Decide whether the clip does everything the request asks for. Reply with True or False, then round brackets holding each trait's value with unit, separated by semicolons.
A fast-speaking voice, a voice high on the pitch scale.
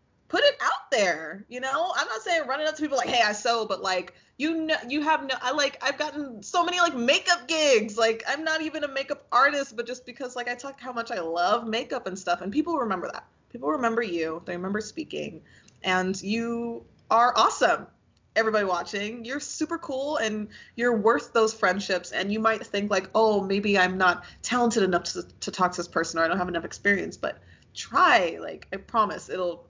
True (215 wpm; 230 Hz)